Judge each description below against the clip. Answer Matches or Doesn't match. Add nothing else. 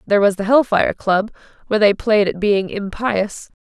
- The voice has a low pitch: Doesn't match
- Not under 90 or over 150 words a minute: Doesn't match